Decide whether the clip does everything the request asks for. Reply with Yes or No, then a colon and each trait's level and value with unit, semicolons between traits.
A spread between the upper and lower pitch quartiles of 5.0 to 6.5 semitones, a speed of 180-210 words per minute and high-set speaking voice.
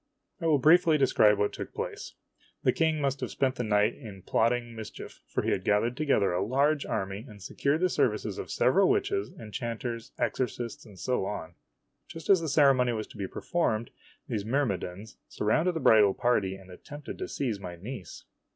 No: wide, 5.5 semitones; average, 185 wpm; low, 120 Hz